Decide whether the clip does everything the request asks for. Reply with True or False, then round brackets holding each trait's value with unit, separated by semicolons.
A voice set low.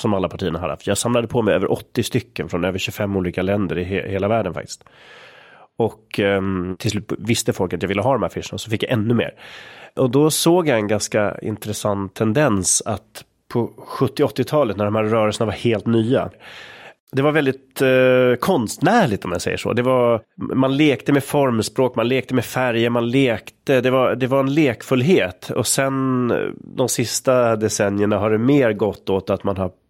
True (115 Hz)